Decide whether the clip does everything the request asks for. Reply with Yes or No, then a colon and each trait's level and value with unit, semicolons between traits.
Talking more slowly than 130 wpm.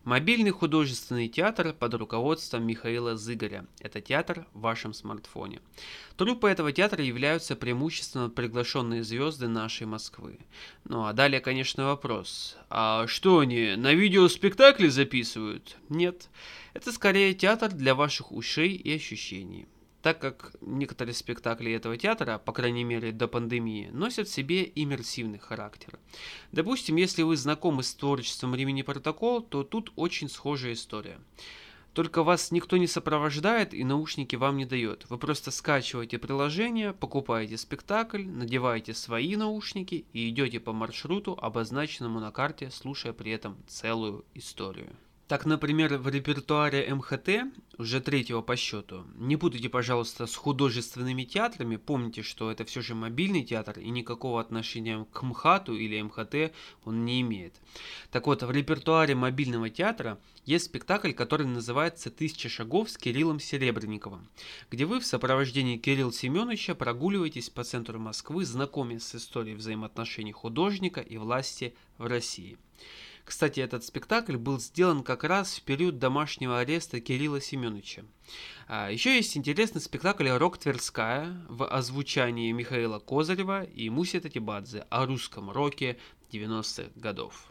No: average, 135 wpm